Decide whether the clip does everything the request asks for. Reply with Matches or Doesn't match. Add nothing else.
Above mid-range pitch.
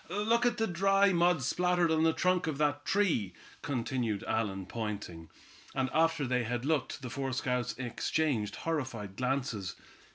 Doesn't match